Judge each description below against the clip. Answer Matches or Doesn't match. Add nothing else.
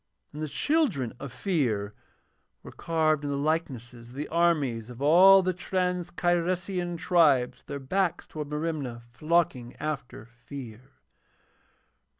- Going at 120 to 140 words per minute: Matches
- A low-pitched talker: Doesn't match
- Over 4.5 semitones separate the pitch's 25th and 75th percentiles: Matches